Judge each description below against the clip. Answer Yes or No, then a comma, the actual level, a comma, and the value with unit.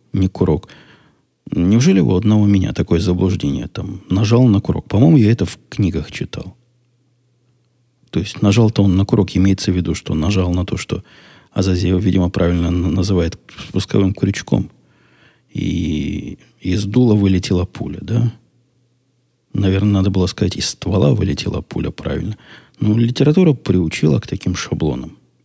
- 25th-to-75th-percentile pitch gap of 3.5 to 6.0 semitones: Yes, average, 4.3 semitones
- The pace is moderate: Yes, average, 140 wpm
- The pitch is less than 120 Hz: Yes, very low, 95 Hz